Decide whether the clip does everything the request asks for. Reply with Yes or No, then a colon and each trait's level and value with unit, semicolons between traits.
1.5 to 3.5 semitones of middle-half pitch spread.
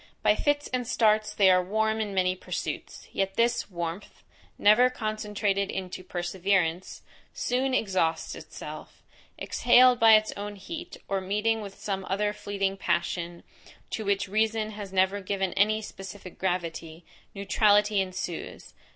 Yes: narrow, 2.5 semitones